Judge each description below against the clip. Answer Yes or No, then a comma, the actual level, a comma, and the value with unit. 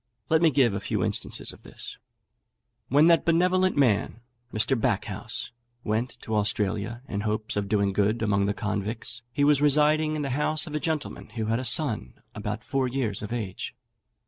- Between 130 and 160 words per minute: No, average, 180 wpm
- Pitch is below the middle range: Yes, low, 120 Hz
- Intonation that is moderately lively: No, wide, 5.9 semitones